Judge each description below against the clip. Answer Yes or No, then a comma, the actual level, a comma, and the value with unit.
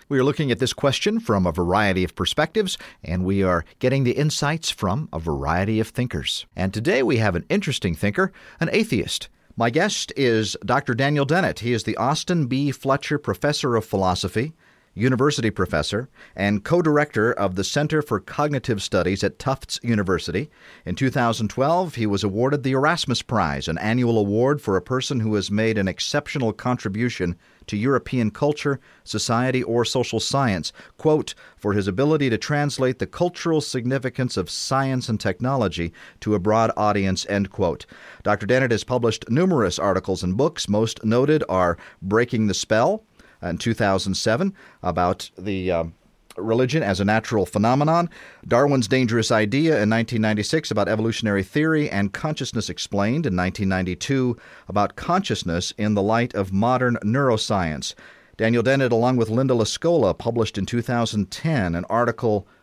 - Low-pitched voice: Yes, low, 115 Hz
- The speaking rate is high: No, average, 155 wpm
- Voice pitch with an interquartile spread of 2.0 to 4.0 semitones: No, average, 5.3 semitones